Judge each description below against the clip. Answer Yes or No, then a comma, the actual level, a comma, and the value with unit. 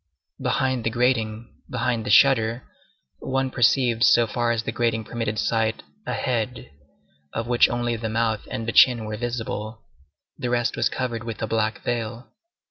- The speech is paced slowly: No, average, 165 wpm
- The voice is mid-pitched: No, low, 115 Hz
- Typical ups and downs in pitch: No, narrow, 1.5 semitones